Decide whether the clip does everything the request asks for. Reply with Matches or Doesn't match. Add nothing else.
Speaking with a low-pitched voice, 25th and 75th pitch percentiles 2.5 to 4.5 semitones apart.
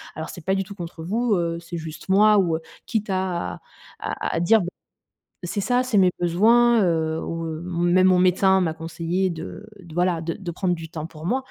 Doesn't match